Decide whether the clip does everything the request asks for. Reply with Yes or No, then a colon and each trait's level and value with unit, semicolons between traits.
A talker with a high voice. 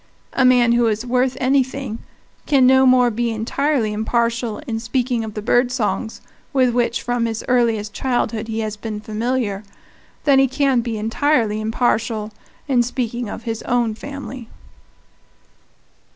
Yes: high, 240 Hz